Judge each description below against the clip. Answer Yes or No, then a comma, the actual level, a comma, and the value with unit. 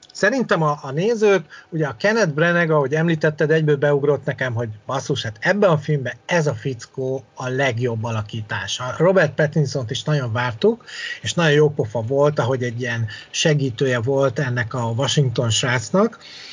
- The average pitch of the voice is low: No, medium, 145 Hz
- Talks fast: Yes, fast, 165 wpm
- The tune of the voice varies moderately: Yes, average, 4.1 semitones